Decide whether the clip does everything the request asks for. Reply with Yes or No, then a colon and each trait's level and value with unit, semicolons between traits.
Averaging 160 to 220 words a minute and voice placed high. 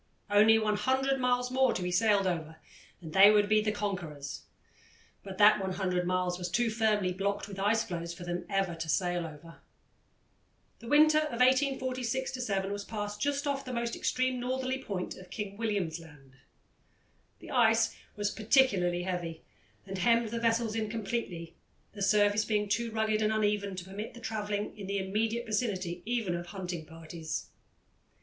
Yes: average, 170 wpm; high, 205 Hz